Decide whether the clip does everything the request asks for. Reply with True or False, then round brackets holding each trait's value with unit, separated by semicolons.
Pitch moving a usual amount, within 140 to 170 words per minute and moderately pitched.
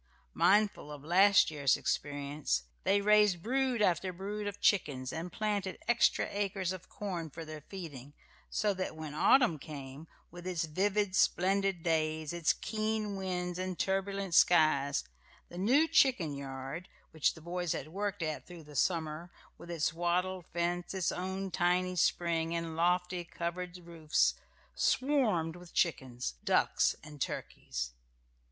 True (3.6 semitones; 145 wpm; 175 Hz)